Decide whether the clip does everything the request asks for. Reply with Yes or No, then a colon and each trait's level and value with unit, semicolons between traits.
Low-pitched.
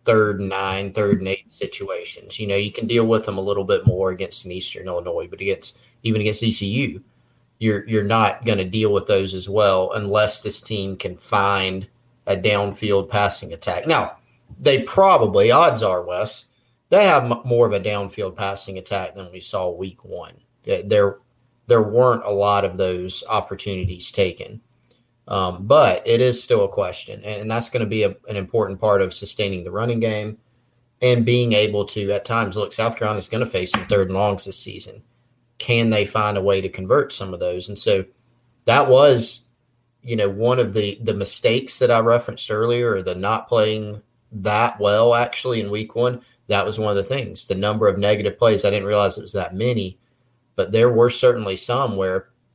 Yes: low, 110 Hz